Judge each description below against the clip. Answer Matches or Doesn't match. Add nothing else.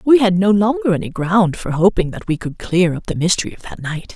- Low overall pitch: Doesn't match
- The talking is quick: Matches